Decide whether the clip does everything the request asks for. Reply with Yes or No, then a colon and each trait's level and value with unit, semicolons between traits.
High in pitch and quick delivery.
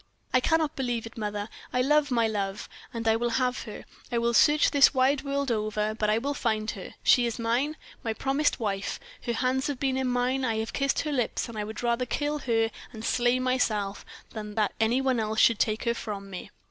Yes: high, 235 Hz; fast, 225 wpm